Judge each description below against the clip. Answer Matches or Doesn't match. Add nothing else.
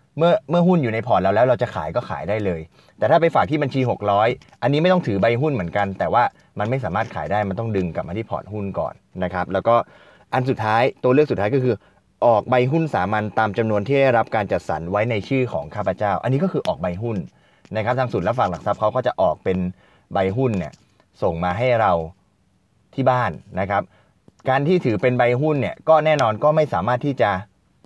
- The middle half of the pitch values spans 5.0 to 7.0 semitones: Matches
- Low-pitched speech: Matches